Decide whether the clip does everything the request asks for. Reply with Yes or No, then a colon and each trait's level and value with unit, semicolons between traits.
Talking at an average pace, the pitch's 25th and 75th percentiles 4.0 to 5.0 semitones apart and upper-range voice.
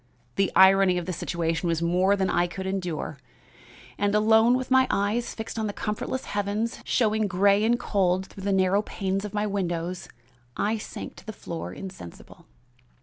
No: average, 175 wpm; narrow, 2.6 semitones; high, 195 Hz